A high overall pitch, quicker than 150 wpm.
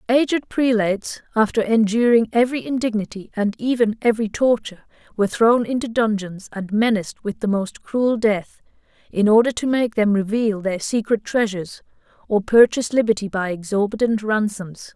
No: high, 220 Hz; average, 145 wpm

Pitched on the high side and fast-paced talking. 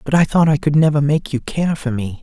No: medium, 145 Hz; fast, 295 wpm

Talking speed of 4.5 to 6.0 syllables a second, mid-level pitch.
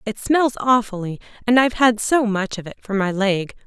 No: 5.2 syllables/s; high, 220 Hz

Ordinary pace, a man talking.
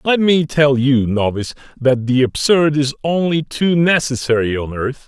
Yes: average, 165 wpm; male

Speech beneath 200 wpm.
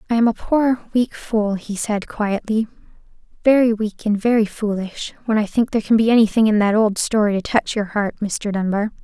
No: fast, 205 wpm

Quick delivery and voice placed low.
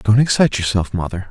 No: average, 185 wpm; low, 105 Hz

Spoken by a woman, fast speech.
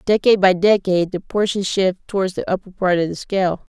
Yes: female; fast, 210 wpm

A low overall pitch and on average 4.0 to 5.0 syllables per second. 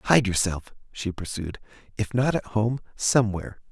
Yes: low, 105 Hz; 4.9 syllables/s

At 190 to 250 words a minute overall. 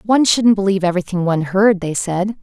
Yes: average, 200 wpm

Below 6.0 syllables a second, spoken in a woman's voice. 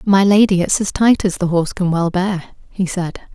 Yes: 5.6 syllables/s; female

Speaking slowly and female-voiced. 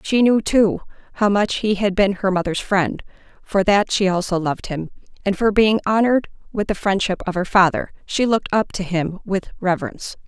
No: average, 200 wpm; female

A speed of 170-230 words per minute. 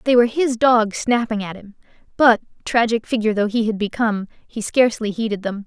Yes: average, 190 wpm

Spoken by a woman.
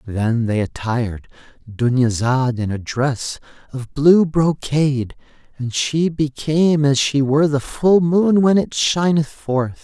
No: male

